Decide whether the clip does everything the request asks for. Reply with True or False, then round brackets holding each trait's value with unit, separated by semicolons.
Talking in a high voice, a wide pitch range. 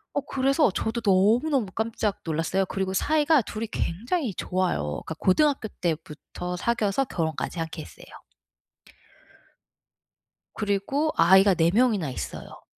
True (200 Hz; 6.0 semitones)